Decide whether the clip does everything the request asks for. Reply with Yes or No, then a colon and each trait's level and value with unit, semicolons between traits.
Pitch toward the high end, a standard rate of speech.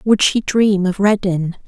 Yes: high, 195 Hz; average, 180 wpm